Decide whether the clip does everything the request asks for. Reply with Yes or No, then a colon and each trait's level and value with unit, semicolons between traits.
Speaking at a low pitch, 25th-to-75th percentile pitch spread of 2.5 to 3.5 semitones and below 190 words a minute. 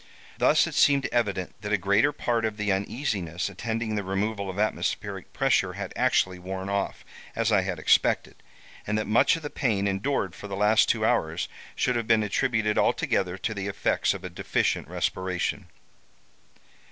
Yes: low, 105 Hz; average, 2.8 semitones; average, 175 wpm